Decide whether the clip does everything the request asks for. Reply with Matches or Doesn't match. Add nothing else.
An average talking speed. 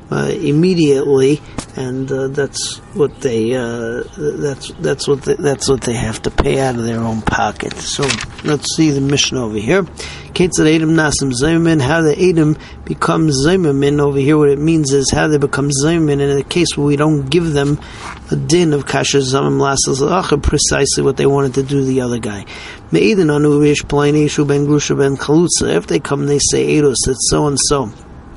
Matches